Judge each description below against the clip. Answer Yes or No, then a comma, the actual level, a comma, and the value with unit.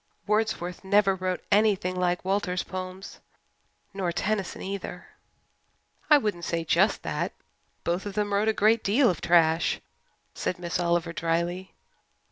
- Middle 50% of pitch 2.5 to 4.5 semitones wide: Yes, average, 2.9 semitones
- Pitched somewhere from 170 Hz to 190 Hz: Yes, medium, 185 Hz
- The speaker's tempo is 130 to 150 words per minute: Yes, slow, 135 wpm